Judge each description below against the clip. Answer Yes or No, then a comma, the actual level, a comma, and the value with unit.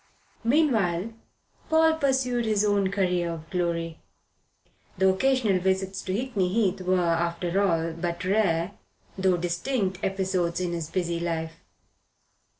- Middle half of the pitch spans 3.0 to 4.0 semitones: Yes, average, 3.4 semitones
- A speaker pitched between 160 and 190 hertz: Yes, medium, 185 Hz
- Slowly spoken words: Yes, slow, 125 wpm